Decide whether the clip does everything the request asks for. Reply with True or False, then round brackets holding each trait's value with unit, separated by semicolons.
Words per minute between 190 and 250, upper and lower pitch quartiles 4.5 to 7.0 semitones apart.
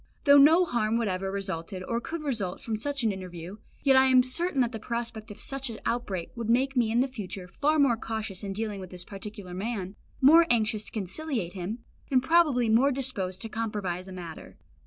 True (205 wpm; 5.1 semitones)